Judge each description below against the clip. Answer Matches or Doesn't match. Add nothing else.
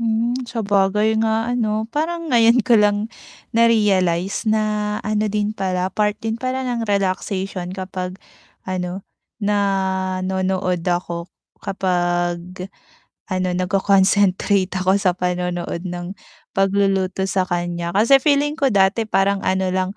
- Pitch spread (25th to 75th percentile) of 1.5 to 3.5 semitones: Matches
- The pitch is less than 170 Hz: Doesn't match